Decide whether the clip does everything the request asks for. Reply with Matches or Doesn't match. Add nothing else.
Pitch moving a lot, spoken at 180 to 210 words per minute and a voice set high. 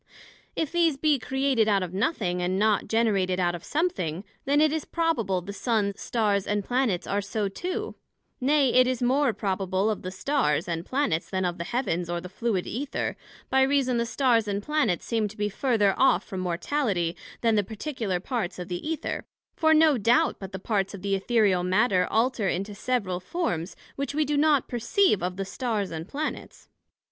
Matches